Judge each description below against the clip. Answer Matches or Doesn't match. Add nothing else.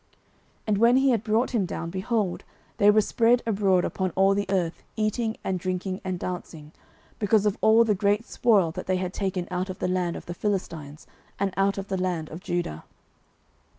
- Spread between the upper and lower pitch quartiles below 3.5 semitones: Matches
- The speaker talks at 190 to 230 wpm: Matches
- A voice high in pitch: Matches